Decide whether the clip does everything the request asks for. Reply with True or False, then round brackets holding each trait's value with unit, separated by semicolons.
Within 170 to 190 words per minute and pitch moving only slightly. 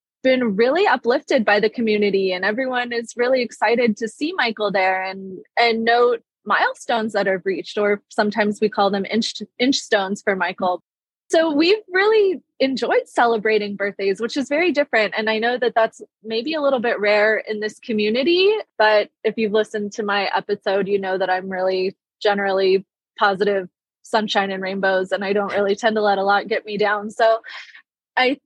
False (185 wpm; 3.3 semitones)